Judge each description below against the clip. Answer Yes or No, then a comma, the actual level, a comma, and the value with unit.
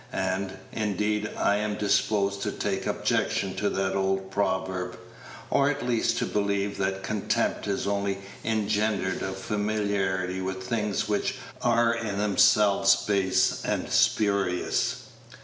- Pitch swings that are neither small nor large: No, narrow, 1.7 semitones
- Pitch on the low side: Yes, low, 100 Hz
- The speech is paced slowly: Yes, slow, 130 wpm